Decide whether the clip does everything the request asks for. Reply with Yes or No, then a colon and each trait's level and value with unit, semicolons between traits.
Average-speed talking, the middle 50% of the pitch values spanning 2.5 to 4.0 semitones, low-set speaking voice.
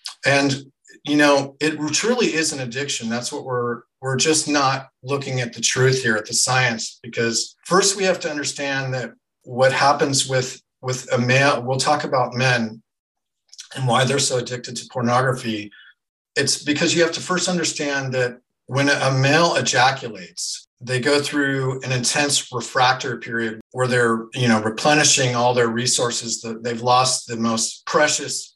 Yes: average, 165 wpm; average, 2.8 semitones; low, 130 Hz